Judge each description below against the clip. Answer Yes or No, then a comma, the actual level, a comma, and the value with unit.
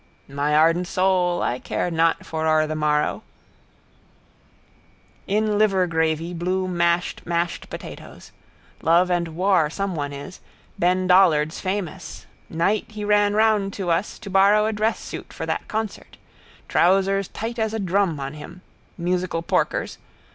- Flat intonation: No, average, 3.2 semitones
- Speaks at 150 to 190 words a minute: No, average, 140 wpm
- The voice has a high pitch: No, medium, 180 Hz